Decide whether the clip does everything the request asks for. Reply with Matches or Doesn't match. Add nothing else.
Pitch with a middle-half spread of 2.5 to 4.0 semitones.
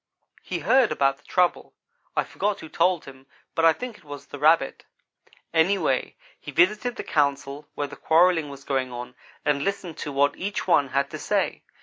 Doesn't match